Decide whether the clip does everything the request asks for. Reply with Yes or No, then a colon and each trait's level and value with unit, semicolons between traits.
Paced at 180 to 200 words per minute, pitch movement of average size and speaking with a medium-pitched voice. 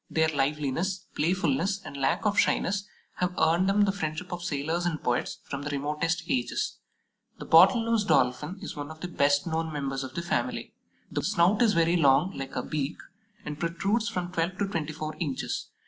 Yes: average, 190 wpm; average, 4.1 semitones; medium, 165 Hz